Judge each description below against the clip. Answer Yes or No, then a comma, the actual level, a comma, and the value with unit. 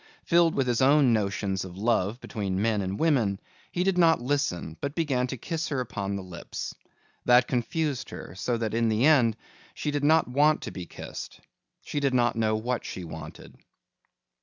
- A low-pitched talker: Yes, low, 120 Hz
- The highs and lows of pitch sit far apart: Yes, wide, 6.2 semitones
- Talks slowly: No, average, 185 wpm